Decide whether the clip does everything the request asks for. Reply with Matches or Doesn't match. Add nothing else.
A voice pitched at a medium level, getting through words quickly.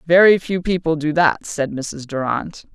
Doesn't match